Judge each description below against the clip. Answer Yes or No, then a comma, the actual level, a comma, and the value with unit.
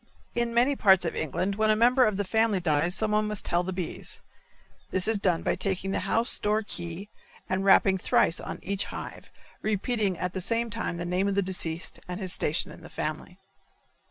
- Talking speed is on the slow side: No, fast, 205 wpm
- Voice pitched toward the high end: Yes, high, 195 Hz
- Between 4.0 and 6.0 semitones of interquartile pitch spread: No, average, 3.2 semitones